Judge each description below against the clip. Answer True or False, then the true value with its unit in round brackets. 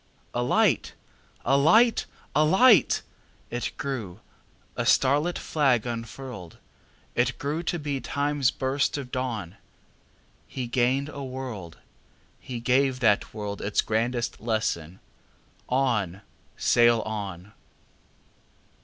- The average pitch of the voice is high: False (125 Hz)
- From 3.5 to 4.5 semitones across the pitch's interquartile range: True (4.2 semitones)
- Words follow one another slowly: True (95 wpm)